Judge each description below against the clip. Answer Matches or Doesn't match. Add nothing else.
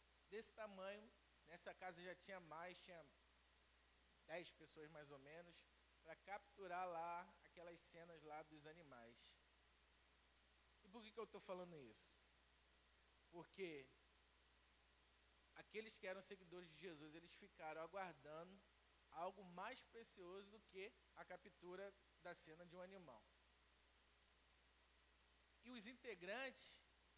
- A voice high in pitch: Doesn't match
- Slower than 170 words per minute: Matches